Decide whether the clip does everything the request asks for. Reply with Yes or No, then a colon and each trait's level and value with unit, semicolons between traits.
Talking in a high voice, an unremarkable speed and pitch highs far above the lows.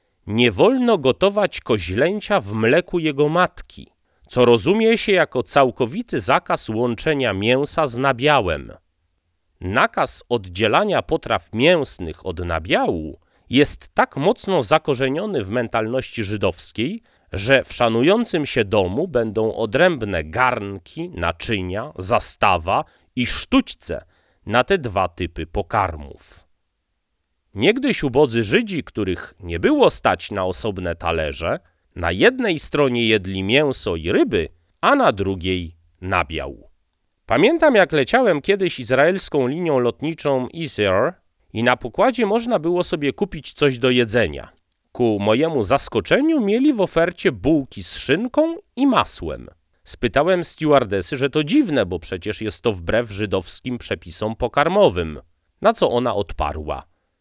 No: low, 120 Hz; average, 120 wpm; wide, 8.7 semitones